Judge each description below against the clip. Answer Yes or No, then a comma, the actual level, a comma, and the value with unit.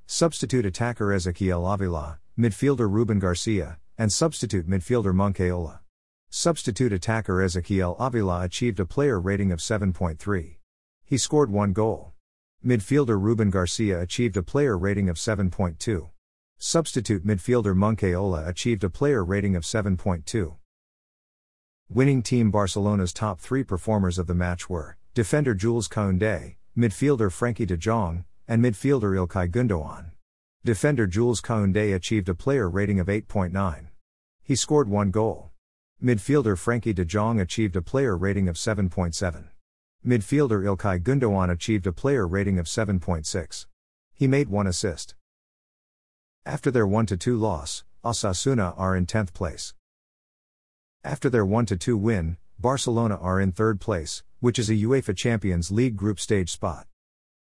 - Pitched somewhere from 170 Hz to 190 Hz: No, low, 100 Hz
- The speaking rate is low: Yes, slow, 130 wpm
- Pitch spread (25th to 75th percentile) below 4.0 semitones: No, average, 4.5 semitones